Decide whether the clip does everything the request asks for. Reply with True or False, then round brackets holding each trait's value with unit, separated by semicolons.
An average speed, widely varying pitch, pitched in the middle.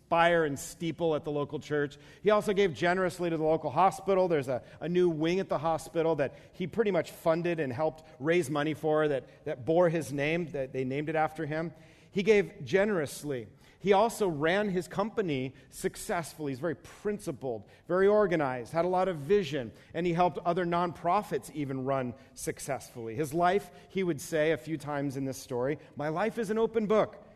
False (195 wpm; 3.8 semitones; 165 Hz)